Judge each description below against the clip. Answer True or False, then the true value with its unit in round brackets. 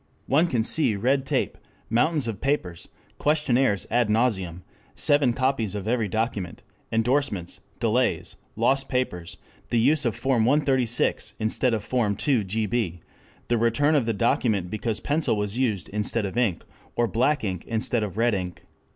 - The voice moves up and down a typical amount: True (4.0 semitones)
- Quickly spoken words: False (150 wpm)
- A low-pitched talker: True (115 Hz)